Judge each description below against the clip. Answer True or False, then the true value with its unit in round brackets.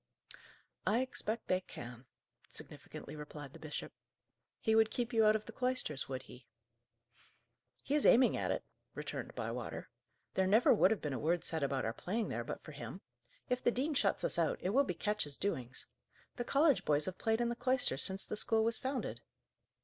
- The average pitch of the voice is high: True (210 Hz)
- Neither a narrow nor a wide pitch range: False (8.3 semitones)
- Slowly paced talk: False (195 wpm)